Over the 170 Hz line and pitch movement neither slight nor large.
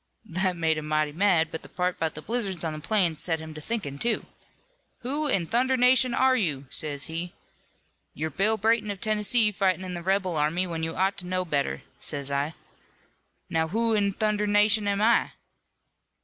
Yes: medium, 185 Hz; average, 5.0 semitones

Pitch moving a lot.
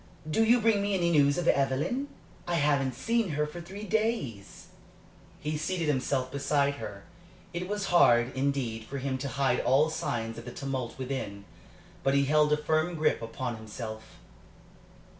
No: average, 4.9 semitones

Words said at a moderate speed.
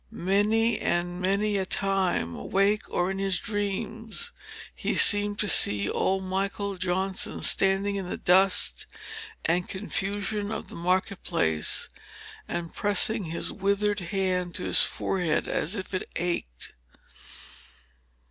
No: slow, 130 wpm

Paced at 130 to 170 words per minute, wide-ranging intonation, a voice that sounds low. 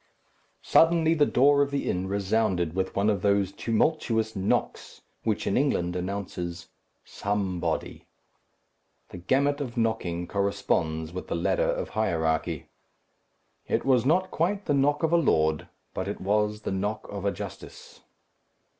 Yes: average, 145 wpm; wide, 6.9 semitones; low, 105 Hz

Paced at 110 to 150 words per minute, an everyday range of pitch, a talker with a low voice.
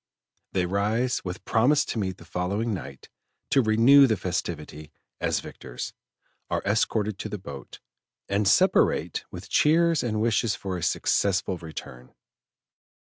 Yes: slow, 135 wpm; average, 4.1 semitones; low, 100 Hz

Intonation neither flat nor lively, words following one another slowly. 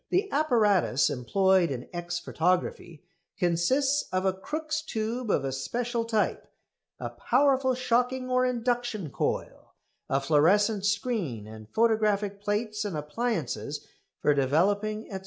No: wide, 6.0 semitones; slow, 125 wpm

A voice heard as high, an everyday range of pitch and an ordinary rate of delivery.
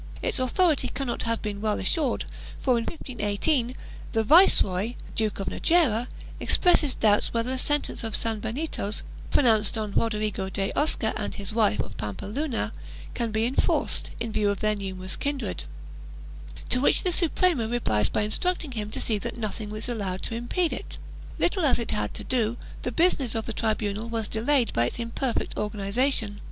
Yes: high, 225 Hz; average, 3.7 semitones; average, 170 wpm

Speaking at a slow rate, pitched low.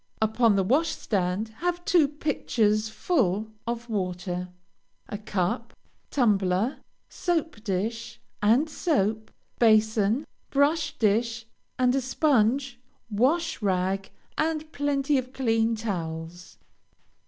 No: slow, 100 wpm; high, 225 Hz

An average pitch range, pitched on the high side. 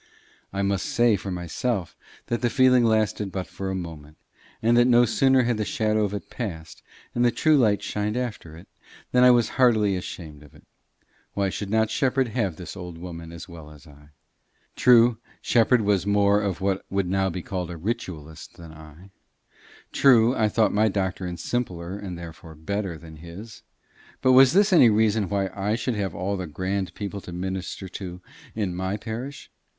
No: average, 4.4 semitones; low, 100 Hz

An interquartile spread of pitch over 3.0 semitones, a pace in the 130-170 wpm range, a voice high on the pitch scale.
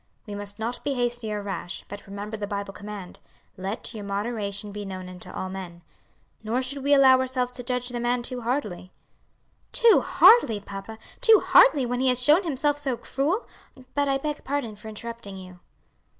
No: average, 4.5 semitones; average, 185 wpm; high, 235 Hz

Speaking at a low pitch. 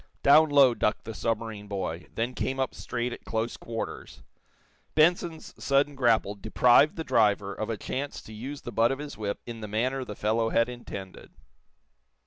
Yes: low, 115 Hz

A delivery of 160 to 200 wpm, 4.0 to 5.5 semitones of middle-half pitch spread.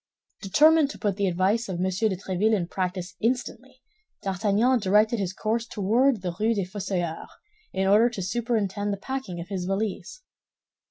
No: average, 165 wpm; average, 3.6 semitones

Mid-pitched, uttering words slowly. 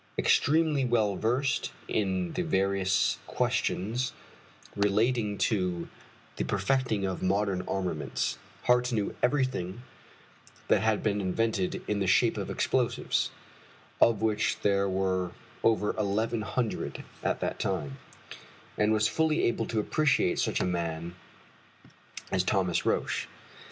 No: low, 105 Hz; slow, 120 wpm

